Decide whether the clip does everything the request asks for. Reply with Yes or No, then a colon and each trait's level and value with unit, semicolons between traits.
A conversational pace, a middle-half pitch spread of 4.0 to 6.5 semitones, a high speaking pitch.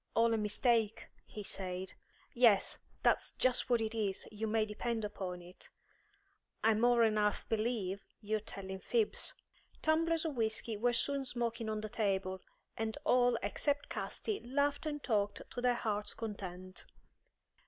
No: average, 145 wpm; average, 3.0 semitones; high, 220 Hz